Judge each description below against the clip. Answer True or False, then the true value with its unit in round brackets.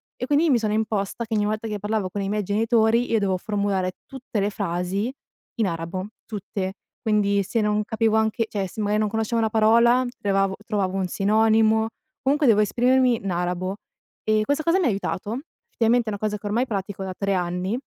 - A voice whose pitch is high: True (210 Hz)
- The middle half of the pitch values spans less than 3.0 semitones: True (2.4 semitones)